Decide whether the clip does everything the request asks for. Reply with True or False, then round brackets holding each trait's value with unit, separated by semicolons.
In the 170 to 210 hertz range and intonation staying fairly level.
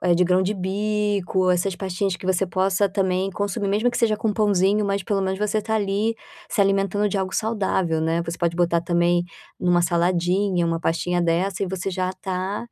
True (190 Hz; 2.3 semitones)